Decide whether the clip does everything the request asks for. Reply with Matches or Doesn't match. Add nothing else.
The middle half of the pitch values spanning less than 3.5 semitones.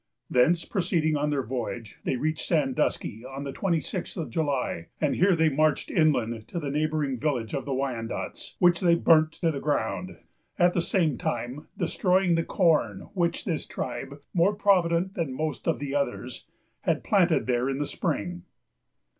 Doesn't match